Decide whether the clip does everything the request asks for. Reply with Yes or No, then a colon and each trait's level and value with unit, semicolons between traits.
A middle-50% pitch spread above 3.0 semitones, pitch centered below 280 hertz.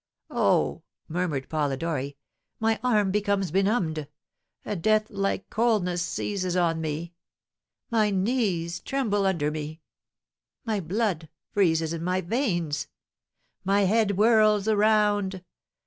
Yes: average, 4.3 semitones; high, 190 Hz